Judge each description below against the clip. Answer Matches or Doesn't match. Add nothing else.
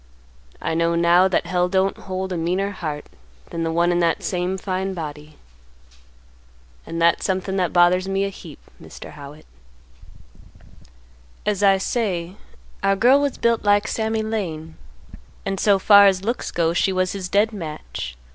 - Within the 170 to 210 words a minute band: Doesn't match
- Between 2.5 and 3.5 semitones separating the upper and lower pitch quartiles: Matches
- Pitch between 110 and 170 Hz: Doesn't match